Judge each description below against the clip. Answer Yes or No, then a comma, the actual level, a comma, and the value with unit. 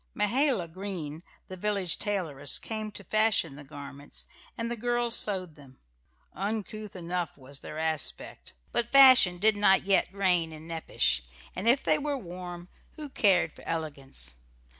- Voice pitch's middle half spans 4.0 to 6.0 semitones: Yes, average, 5.3 semitones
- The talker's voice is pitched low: No, medium, 185 Hz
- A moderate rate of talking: Yes, average, 150 wpm